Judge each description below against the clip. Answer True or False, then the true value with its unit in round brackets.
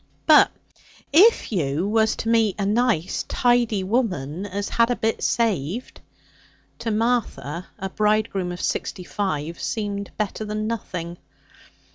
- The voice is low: False (210 Hz)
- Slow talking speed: True (130 wpm)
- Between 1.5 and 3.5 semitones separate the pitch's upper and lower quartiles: False (3.9 semitones)